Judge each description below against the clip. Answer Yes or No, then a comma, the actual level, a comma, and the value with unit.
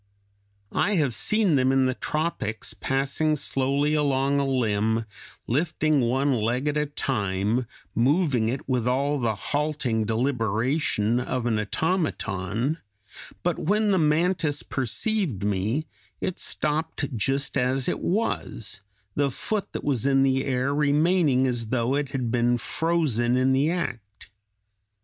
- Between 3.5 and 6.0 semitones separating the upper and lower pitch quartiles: Yes, average, 4.2 semitones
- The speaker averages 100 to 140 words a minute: Yes, slow, 135 wpm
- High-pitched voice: No, low, 135 Hz